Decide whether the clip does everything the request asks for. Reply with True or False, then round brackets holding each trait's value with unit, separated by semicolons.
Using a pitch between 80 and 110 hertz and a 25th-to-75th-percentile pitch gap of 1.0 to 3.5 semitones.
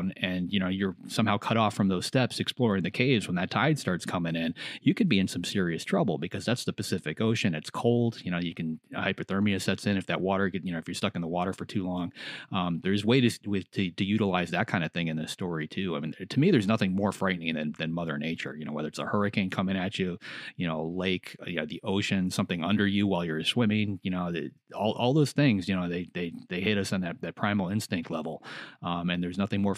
True (95 Hz; 2.8 semitones)